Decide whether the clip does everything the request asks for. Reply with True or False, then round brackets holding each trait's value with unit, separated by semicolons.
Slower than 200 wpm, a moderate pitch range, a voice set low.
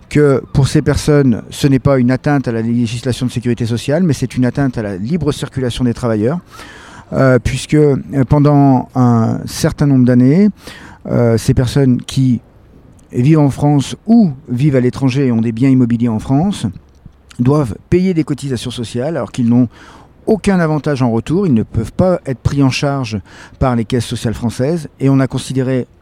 True (180 wpm; 3.2 semitones; 130 Hz)